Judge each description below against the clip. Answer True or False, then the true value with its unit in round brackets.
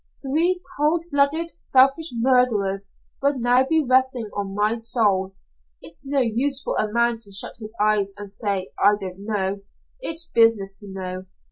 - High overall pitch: True (230 Hz)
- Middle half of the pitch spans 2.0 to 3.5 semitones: False (5.3 semitones)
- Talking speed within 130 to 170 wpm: True (160 wpm)